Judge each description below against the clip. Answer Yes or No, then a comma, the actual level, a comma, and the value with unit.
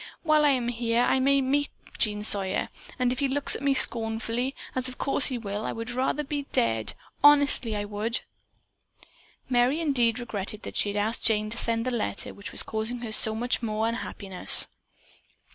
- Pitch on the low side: No, high, 235 Hz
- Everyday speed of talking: Yes, average, 185 wpm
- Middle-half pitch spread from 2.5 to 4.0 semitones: Yes, average, 3.4 semitones